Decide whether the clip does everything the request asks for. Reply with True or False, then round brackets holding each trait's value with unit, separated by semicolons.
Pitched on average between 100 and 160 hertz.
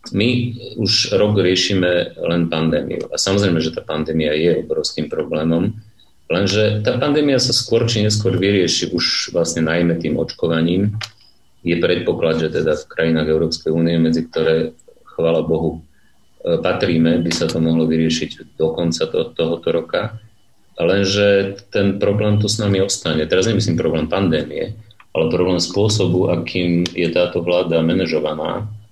False (90 Hz)